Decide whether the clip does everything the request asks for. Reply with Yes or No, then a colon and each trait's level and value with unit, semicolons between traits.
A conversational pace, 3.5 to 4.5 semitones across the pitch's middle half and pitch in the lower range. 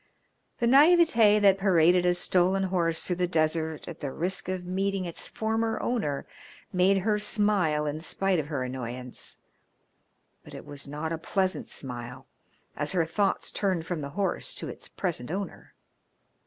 No: average, 160 wpm; average, 4.2 semitones; medium, 180 Hz